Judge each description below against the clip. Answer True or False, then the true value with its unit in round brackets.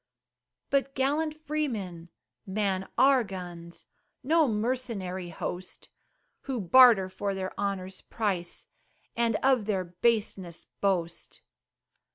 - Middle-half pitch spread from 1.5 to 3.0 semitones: False (5.6 semitones)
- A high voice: True (200 Hz)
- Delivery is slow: True (100 wpm)